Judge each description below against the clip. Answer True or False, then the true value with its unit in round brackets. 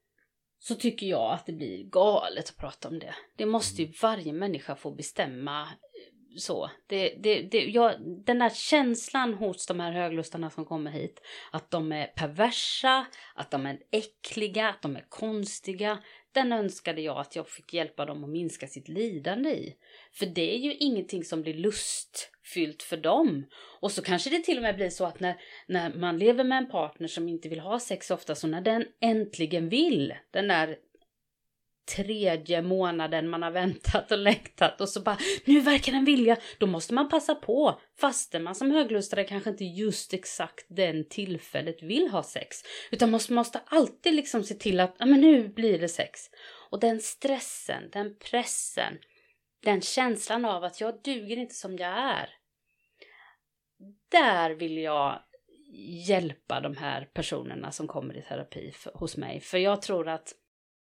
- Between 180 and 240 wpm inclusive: False (170 wpm)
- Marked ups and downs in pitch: True (5.9 semitones)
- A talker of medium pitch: False (200 Hz)